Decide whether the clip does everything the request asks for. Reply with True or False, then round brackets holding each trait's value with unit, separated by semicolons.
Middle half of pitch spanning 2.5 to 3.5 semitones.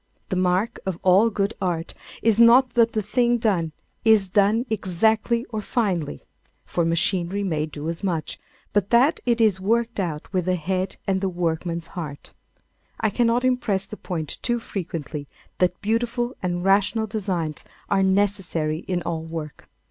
False (4.5 semitones)